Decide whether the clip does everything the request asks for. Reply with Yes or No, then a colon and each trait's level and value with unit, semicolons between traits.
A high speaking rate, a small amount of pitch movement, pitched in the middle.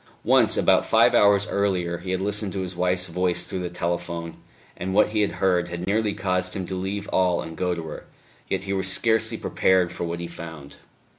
No: fast, 215 wpm; narrow, 2.2 semitones; very low, 90 Hz